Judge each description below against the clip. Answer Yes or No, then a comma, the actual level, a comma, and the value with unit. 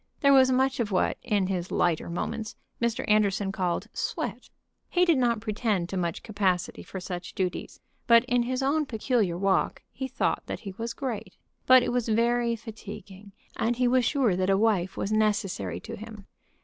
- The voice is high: Yes, high, 215 Hz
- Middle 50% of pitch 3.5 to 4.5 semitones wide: Yes, average, 4.1 semitones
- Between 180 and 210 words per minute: Yes, average, 185 wpm